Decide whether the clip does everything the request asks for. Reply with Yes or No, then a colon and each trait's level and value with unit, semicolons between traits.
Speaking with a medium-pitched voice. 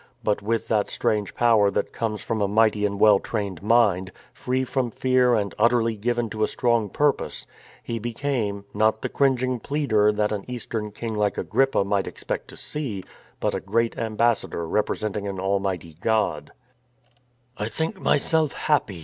No: low, 110 Hz